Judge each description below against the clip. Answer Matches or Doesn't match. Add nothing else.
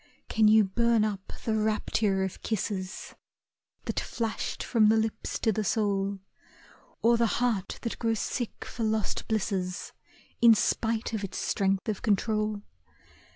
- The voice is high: Matches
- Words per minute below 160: Matches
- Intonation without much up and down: Matches